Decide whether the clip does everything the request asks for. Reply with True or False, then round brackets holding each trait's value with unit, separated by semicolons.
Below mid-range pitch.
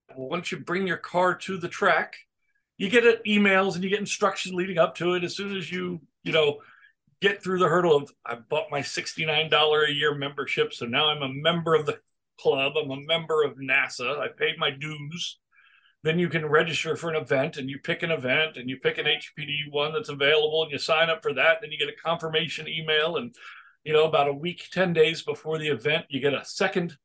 False (160 Hz)